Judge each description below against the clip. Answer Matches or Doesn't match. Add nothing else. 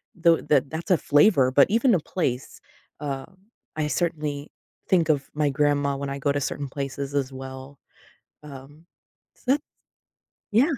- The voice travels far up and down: Doesn't match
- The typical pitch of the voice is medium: Matches